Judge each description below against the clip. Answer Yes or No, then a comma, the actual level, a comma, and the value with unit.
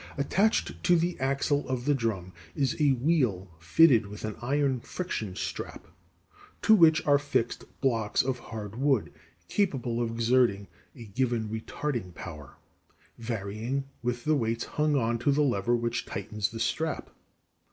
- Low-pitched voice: Yes, low, 120 Hz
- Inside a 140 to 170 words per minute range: Yes, average, 150 wpm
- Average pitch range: Yes, average, 4.4 semitones